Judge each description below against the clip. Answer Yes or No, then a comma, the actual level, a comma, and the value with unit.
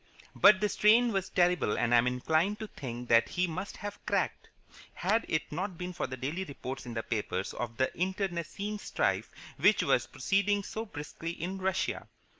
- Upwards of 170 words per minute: Yes, average, 185 wpm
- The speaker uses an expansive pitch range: Yes, wide, 7.3 semitones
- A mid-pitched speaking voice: Yes, medium, 180 Hz